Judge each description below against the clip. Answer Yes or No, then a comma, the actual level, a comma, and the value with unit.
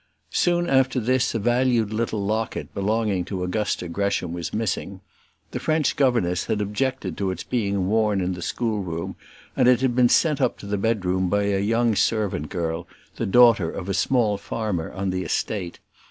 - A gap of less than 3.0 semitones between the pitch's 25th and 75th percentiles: No, average, 4.2 semitones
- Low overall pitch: Yes, low, 105 Hz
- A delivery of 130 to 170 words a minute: No, average, 180 wpm